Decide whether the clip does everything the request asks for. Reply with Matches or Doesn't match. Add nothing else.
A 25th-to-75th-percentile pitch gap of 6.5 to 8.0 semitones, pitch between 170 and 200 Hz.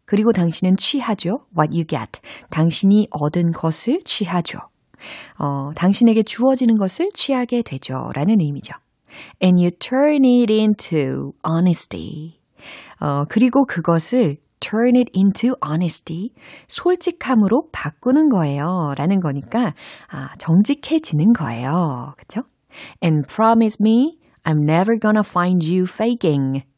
Matches